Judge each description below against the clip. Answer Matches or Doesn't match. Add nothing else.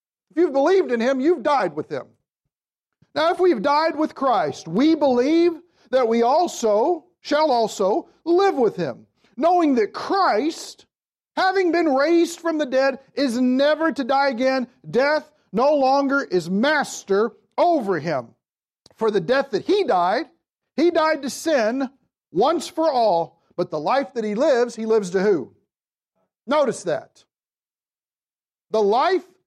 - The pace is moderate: Matches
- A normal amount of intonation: Doesn't match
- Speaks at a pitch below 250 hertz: Doesn't match